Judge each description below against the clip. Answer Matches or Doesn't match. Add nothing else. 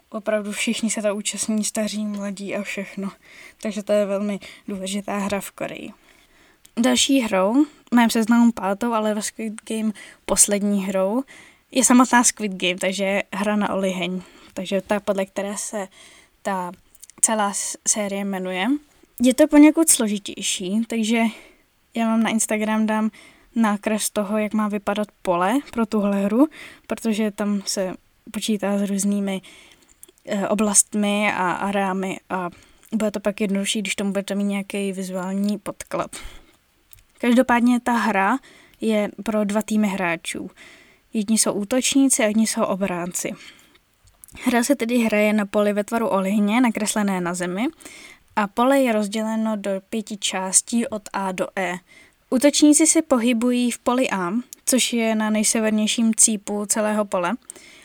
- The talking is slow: Doesn't match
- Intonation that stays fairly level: Doesn't match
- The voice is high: Matches